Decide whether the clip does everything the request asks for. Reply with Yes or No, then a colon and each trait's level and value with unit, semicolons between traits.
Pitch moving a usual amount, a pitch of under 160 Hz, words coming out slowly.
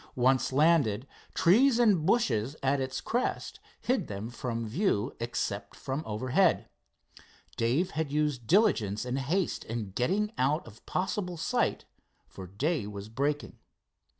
No: wide, 7.4 semitones; low, 135 Hz; slow, 130 wpm